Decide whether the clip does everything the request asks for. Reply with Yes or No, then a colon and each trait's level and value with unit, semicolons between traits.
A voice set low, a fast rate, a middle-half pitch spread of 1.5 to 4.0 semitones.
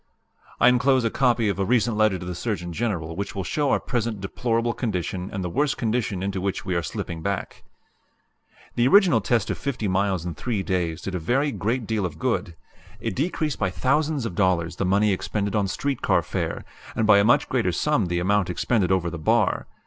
No: low, 100 Hz; fast, 210 wpm; average, 4.7 semitones